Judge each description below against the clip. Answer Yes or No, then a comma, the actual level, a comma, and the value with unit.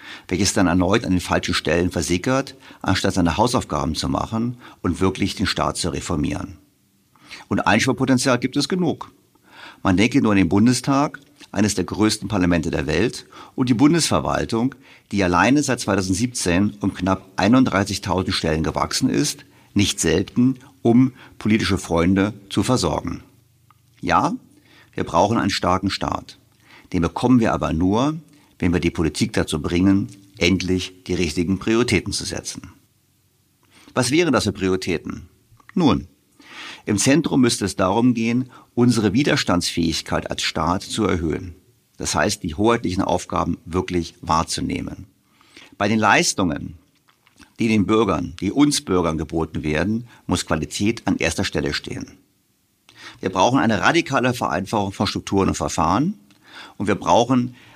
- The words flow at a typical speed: Yes, average, 140 wpm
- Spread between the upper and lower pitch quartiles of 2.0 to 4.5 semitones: No, average, 5.2 semitones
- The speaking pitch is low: Yes, very low, 95 Hz